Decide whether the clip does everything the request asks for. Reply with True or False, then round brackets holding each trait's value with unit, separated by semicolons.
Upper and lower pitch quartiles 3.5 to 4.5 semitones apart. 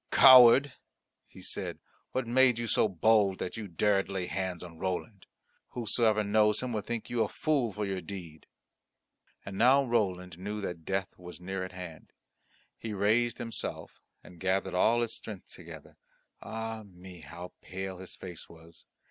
True (3.9 semitones)